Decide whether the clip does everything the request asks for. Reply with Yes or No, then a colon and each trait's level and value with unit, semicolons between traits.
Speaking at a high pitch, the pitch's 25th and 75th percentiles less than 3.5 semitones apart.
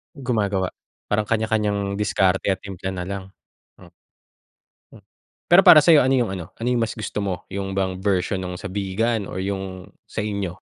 No: low, 100 Hz; average, 2.8 semitones